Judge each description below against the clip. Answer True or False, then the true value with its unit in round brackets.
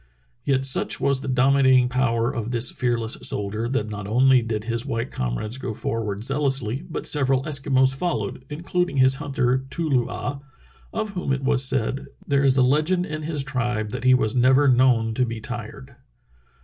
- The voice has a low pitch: True (130 Hz)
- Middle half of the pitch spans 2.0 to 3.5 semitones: True (2.9 semitones)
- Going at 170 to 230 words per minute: True (180 wpm)